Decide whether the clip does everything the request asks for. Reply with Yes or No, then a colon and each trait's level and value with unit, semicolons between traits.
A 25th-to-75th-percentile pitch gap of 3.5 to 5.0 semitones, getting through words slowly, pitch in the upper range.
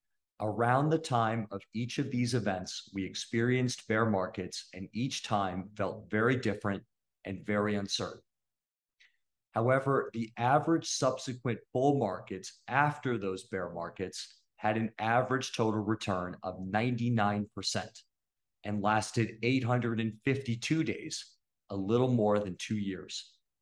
No: average, 3.9 semitones; slow, 120 wpm; low, 110 Hz